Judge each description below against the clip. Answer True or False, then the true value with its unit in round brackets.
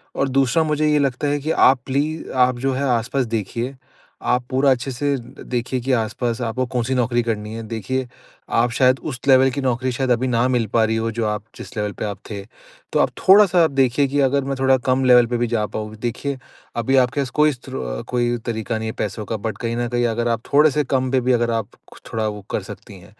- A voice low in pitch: True (125 Hz)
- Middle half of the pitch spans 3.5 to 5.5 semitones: False (2.6 semitones)